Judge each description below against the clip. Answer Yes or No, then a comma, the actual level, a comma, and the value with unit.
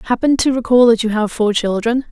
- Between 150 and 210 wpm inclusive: No, fast, 225 wpm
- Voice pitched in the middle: No, high, 230 Hz